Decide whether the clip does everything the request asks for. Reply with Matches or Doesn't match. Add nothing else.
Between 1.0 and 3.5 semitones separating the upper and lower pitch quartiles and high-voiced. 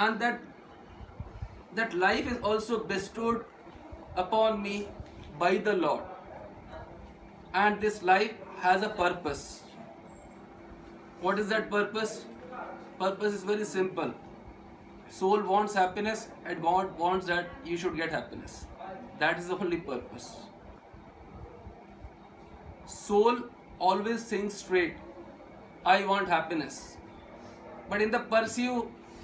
Matches